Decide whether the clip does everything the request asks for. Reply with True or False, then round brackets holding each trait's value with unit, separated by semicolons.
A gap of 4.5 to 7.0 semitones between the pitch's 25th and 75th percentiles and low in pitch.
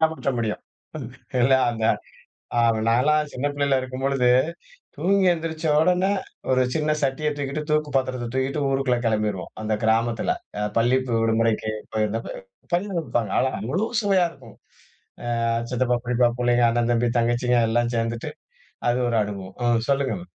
False (3.9 semitones; 125 Hz)